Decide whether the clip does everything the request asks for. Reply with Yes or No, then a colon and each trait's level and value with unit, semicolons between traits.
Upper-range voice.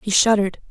Yes: high, 205 Hz